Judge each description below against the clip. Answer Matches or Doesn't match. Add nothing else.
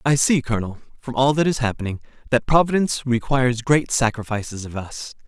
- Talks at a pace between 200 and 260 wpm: Doesn't match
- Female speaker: Doesn't match